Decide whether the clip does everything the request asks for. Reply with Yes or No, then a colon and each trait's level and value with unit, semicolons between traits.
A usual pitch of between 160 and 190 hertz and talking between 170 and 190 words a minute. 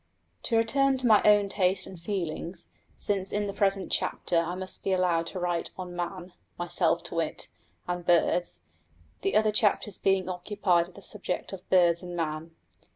Yes: medium, 185 Hz; average, 175 wpm